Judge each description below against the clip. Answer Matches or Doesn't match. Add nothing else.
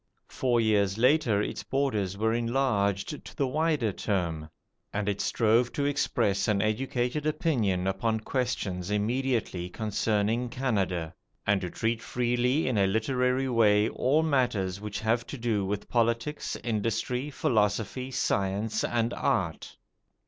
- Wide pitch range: Doesn't match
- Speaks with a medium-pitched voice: Doesn't match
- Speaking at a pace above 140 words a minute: Doesn't match